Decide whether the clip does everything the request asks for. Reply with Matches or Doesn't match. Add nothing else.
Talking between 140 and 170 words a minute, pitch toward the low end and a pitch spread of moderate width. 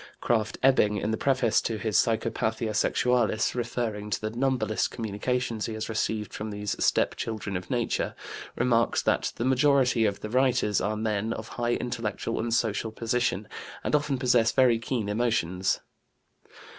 Doesn't match